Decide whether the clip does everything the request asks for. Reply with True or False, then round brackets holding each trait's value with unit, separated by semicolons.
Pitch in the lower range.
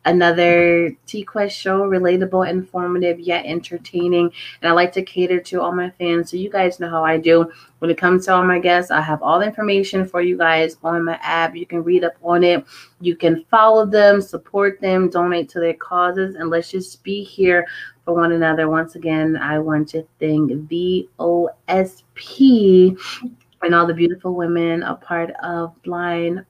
False (175 Hz)